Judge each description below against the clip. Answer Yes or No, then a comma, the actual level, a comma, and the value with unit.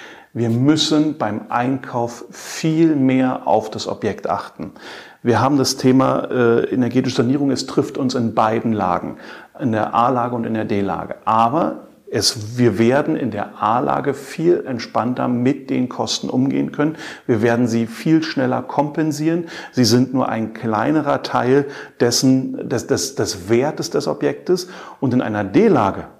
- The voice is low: Yes, low, 125 Hz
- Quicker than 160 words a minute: No, average, 145 wpm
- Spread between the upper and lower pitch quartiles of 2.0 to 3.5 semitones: Yes, average, 3.1 semitones